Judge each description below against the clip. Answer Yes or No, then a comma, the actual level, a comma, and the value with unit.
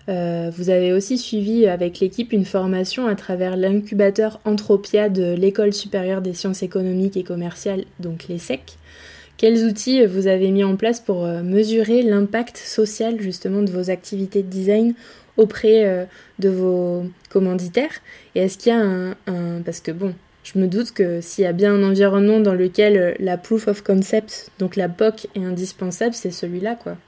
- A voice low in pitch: No, high, 195 Hz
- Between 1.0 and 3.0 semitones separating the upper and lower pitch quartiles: Yes, average, 2.7 semitones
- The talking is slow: No, average, 175 wpm